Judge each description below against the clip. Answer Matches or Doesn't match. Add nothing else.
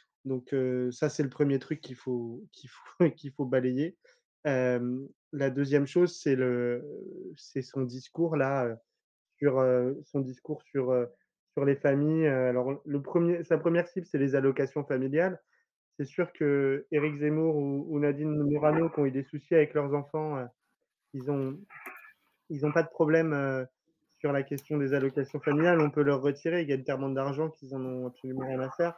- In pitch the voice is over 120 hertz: Matches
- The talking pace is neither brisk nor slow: Matches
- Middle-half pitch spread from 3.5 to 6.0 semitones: Doesn't match